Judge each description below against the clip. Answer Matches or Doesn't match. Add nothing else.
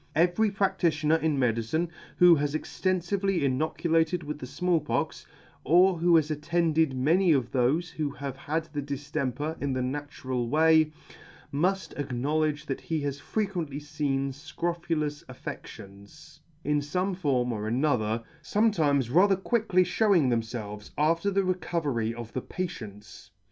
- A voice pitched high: Doesn't match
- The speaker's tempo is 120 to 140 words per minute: Matches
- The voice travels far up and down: Doesn't match